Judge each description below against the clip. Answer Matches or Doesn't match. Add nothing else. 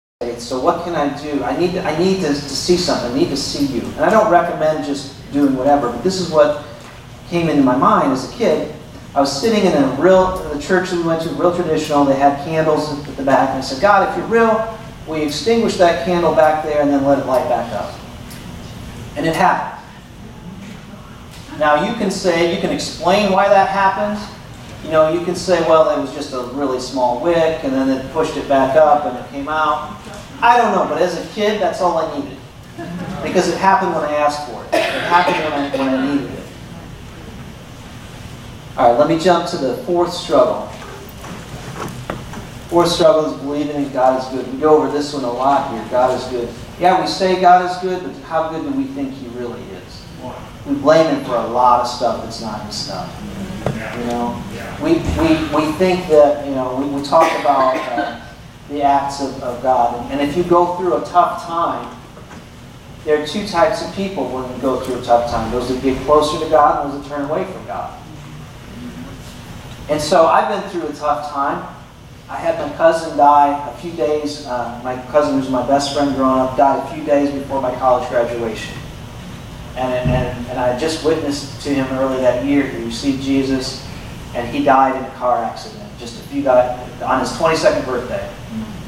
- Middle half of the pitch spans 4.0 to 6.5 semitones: Matches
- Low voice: Doesn't match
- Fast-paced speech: Matches